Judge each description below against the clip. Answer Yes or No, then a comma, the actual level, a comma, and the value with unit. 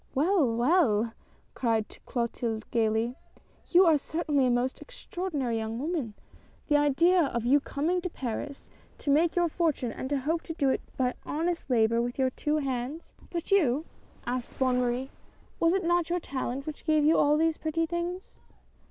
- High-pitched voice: Yes, very high, 285 Hz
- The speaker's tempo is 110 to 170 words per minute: No, average, 185 wpm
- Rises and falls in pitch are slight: No, average, 5.2 semitones